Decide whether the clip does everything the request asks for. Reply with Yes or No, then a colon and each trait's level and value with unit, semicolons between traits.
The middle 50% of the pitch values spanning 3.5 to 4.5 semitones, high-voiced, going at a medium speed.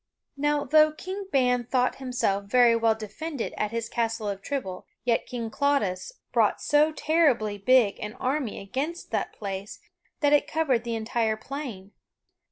No: average, 5.1 semitones; high, 245 Hz; average, 155 wpm